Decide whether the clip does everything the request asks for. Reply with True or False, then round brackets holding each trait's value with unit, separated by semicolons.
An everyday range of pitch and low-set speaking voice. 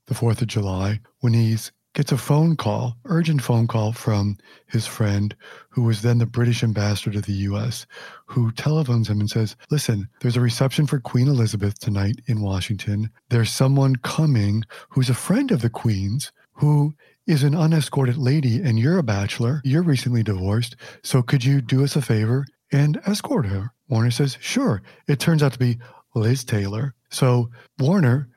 True (4.1 semitones; 120 Hz)